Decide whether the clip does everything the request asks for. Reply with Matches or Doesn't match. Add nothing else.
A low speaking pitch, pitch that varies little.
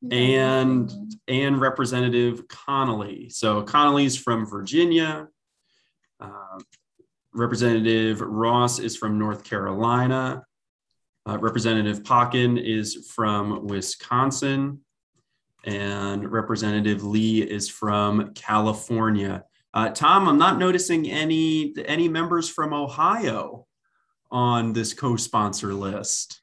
Doesn't match